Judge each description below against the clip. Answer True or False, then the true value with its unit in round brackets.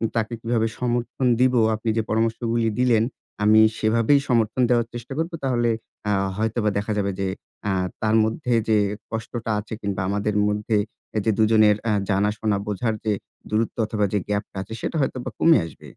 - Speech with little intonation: True (2.0 semitones)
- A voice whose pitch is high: False (110 Hz)